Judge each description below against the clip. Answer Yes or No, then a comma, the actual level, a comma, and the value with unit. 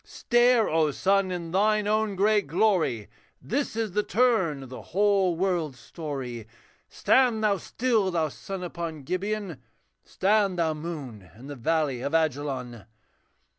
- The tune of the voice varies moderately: No, wide, 6.2 semitones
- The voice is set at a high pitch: No, medium, 175 Hz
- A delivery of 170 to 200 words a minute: No, average, 140 wpm